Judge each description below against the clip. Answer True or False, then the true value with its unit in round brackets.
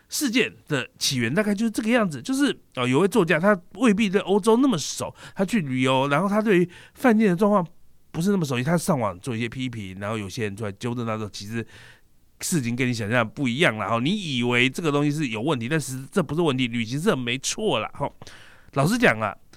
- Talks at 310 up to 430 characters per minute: True (335 characters per minute)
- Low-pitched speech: False (145 Hz)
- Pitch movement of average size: False (8.8 semitones)